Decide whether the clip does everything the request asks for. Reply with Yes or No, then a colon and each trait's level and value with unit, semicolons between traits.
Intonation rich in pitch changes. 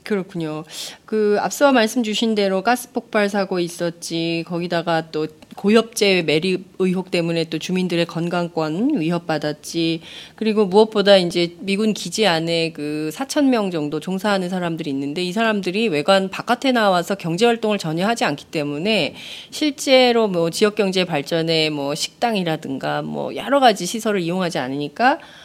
No: average, 4.9 semitones